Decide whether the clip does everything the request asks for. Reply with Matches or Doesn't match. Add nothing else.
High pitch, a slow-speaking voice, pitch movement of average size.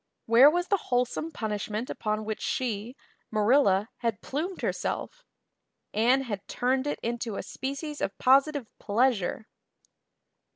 Matches